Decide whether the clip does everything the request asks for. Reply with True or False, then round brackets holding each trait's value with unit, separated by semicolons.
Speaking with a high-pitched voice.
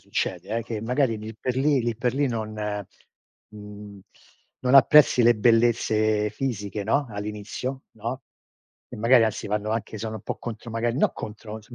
False (110 Hz)